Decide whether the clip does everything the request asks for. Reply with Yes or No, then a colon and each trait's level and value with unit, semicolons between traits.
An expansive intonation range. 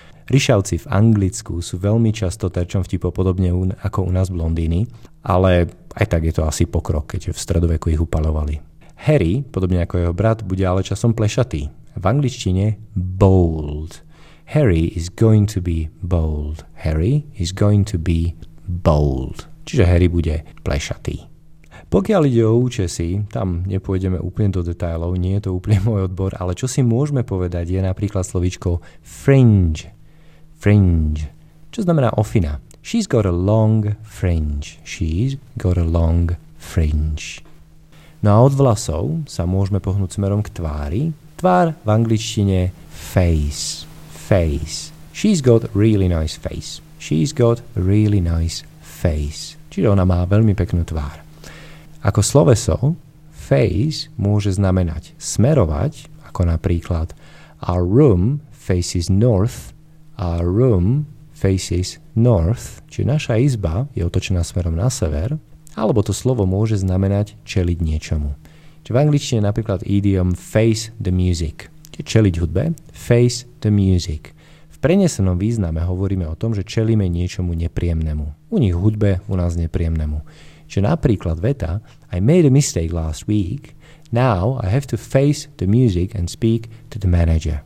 Yes: wide, 5.8 semitones